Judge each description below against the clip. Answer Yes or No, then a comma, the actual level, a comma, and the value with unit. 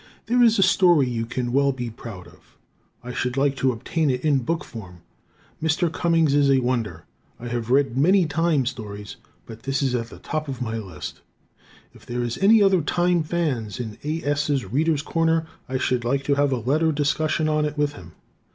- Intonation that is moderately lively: Yes, average, 4.7 semitones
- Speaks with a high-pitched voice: No, medium, 140 Hz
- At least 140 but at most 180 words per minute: No, fast, 205 wpm